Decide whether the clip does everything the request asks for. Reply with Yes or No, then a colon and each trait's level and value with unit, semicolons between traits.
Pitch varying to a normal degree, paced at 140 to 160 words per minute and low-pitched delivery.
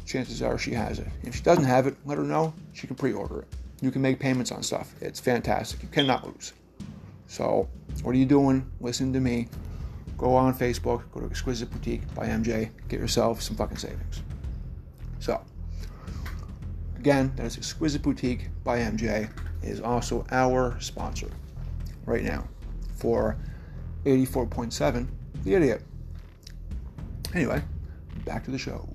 No: wide, 7.8 semitones; average, 155 wpm; low, 115 Hz